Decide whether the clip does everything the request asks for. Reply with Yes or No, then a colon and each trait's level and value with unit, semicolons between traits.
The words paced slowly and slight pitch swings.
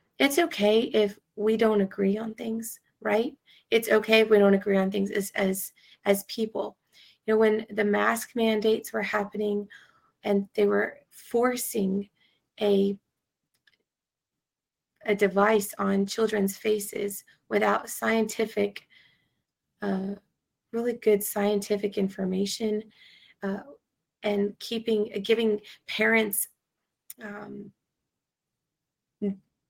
Yes: slow, 105 wpm; narrow, 1.6 semitones